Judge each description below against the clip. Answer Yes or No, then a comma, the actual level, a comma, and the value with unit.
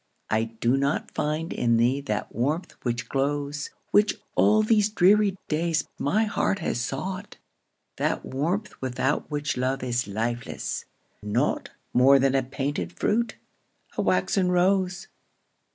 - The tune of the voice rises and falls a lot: Yes, wide, 7.0 semitones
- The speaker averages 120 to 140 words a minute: Yes, slow, 135 wpm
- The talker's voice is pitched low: No, medium, 145 Hz